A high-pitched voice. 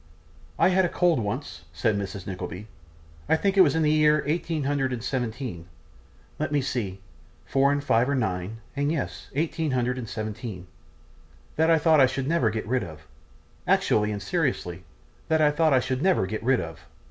No: low, 130 Hz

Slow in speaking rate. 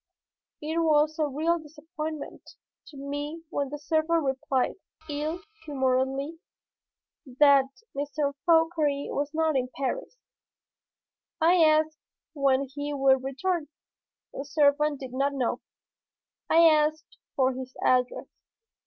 Yes: slow, 115 wpm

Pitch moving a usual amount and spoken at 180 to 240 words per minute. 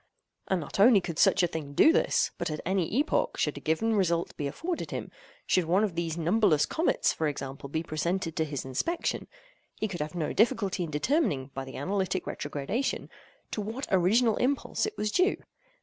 No: wide, 6.5 semitones; average, 185 wpm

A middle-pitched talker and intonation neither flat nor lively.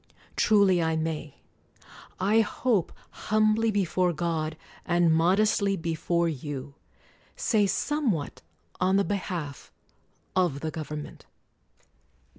Yes: medium, 175 Hz; average, 4.2 semitones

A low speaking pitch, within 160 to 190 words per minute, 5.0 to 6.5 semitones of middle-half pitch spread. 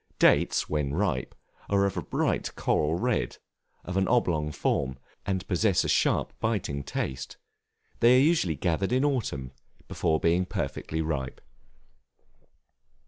No: very low, 90 Hz; slow, 135 wpm; wide, 5.6 semitones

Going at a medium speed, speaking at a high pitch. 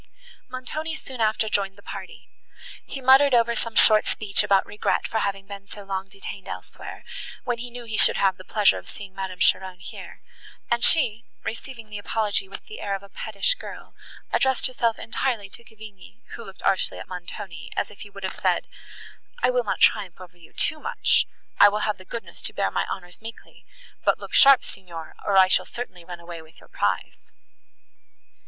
Yes: average, 195 wpm; high, 205 Hz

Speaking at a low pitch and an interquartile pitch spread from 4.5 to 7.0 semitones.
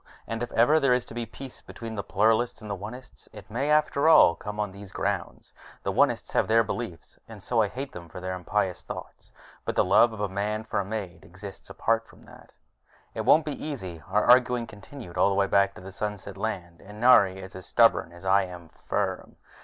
No: low, 105 Hz; average, 3.7 semitones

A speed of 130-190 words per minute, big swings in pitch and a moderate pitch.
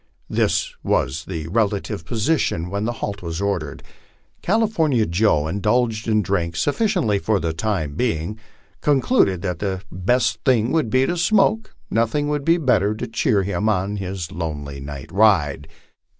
No: average, 160 wpm; wide, 6.6 semitones; low, 105 Hz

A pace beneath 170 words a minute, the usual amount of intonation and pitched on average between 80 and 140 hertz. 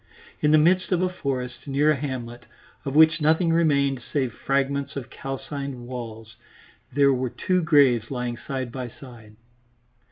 Yes: average, 155 wpm; average, 3.4 semitones; low, 135 Hz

